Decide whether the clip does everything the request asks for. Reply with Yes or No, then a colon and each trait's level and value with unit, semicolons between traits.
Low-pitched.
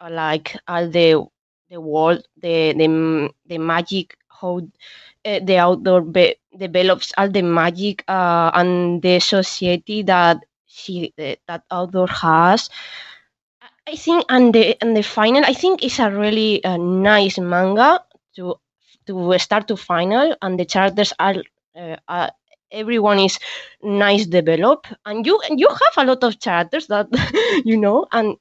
No: high, 190 Hz